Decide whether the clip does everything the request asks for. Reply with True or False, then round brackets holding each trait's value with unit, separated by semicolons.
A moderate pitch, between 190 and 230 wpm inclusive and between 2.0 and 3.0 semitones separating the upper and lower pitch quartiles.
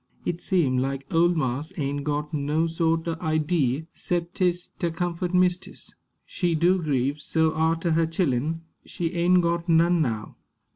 False (165 Hz; 155 wpm; 2.6 semitones)